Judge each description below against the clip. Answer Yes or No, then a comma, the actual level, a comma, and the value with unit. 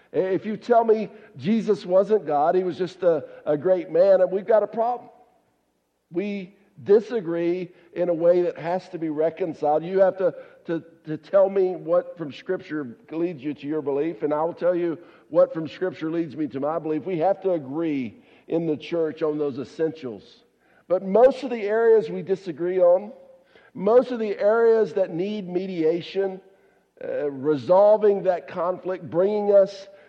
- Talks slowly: No, average, 175 wpm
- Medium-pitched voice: Yes, medium, 180 Hz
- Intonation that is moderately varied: Yes, average, 4.2 semitones